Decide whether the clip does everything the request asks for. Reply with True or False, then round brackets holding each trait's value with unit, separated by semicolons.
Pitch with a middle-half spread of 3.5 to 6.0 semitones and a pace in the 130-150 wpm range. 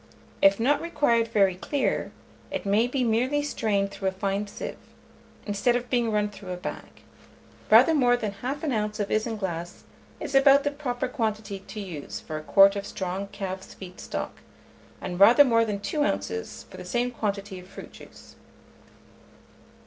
False (3.9 semitones; 170 wpm)